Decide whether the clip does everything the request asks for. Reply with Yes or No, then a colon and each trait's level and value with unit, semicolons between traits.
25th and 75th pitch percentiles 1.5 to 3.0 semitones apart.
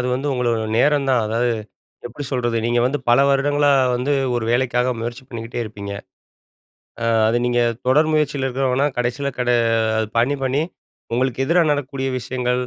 Yes: narrow, 2.6 semitones